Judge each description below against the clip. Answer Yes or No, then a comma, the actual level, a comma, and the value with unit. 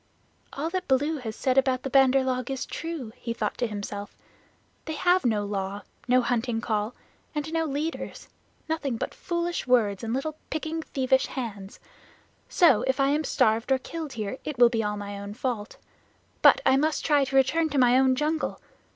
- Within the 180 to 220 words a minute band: Yes, average, 185 wpm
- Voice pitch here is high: Yes, very high, 260 Hz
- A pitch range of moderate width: Yes, average, 4.9 semitones